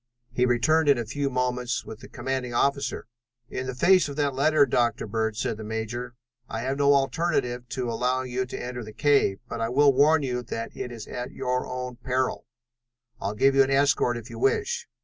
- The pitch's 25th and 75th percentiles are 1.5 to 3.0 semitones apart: Yes, average, 2.7 semitones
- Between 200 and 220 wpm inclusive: Yes, fast, 205 wpm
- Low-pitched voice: Yes, low, 125 Hz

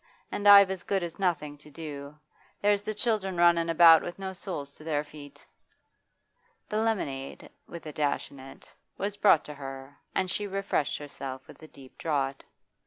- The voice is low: No, medium, 165 Hz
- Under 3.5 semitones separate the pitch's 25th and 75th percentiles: No, average, 5.2 semitones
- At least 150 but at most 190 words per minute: Yes, average, 175 wpm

